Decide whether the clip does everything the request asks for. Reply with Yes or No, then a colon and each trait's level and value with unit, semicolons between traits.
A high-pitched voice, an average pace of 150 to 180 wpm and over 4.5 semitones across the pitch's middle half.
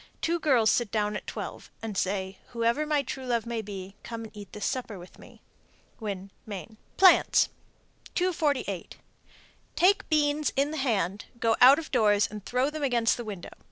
Yes: high, 230 Hz; average, 175 wpm; wide, 5.5 semitones